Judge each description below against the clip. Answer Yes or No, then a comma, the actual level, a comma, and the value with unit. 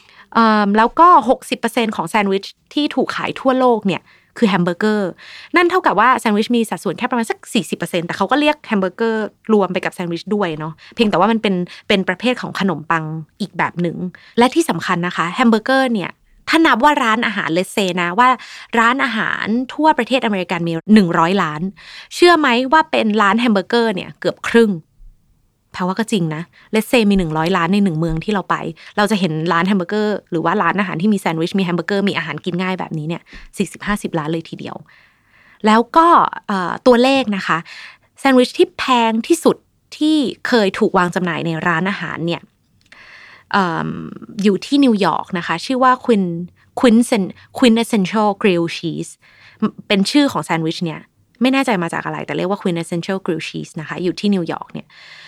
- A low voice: No, high, 205 Hz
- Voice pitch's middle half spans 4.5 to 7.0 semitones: Yes, average, 5.2 semitones